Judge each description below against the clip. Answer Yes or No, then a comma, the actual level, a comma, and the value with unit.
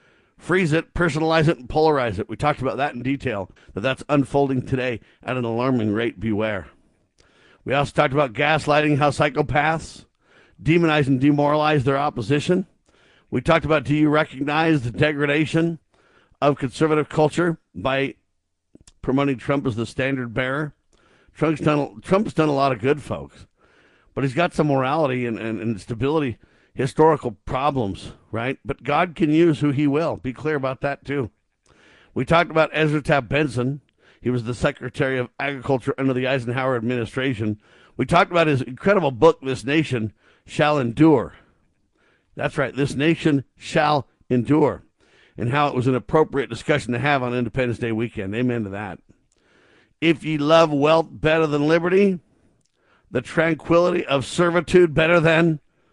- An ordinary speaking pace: Yes, average, 155 wpm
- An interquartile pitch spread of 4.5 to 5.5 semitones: No, average, 3.8 semitones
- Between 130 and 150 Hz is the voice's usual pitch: Yes, medium, 140 Hz